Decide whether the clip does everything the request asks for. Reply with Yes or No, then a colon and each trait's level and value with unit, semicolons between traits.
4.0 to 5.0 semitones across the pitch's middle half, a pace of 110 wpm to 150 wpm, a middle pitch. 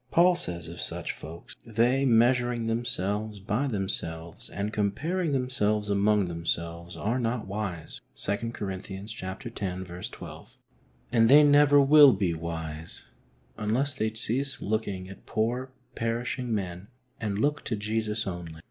No: average, 4.7 semitones; average, 140 wpm; low, 105 Hz